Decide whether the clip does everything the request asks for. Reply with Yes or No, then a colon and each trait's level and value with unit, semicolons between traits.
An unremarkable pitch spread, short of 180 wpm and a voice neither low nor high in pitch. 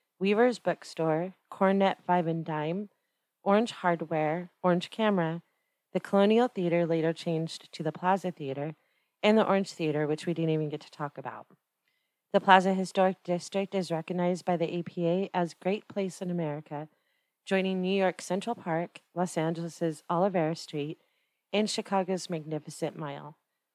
Yes: average, 3.1 semitones; average, 145 wpm; medium, 175 Hz